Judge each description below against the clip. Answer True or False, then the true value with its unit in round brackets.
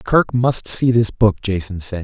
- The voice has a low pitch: True (110 Hz)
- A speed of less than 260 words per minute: True (205 wpm)